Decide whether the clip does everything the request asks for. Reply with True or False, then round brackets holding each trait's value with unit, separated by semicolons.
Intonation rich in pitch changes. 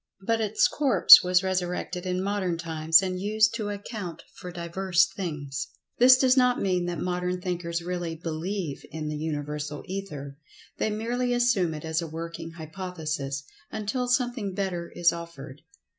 False (3.8 semitones)